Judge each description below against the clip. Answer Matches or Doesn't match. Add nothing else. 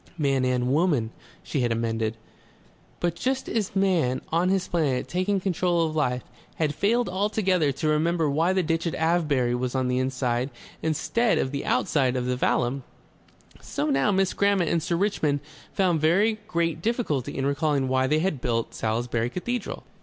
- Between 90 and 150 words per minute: Doesn't match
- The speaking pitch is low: Doesn't match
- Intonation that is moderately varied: Doesn't match